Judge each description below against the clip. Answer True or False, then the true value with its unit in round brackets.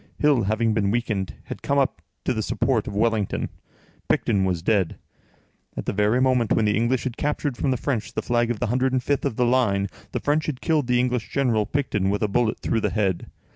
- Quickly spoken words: True (215 wpm)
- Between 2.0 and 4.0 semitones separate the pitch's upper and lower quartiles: True (3.7 semitones)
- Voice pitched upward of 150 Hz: False (115 Hz)